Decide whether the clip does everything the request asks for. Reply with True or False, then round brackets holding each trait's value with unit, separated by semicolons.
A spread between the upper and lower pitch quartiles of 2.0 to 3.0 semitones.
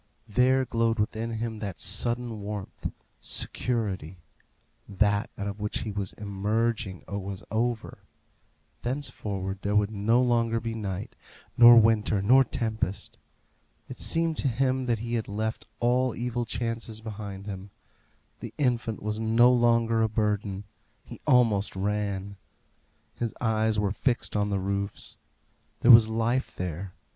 True (2.7 semitones)